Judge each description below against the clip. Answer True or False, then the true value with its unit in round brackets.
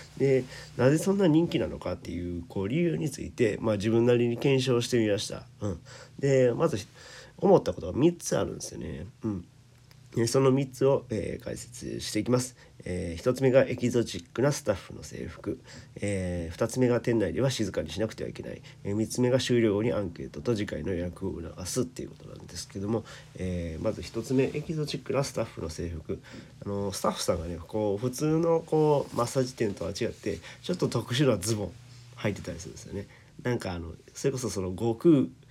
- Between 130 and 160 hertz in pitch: False (120 Hz)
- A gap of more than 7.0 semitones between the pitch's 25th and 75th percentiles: False (5.1 semitones)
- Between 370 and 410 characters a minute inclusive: True (375 characters per minute)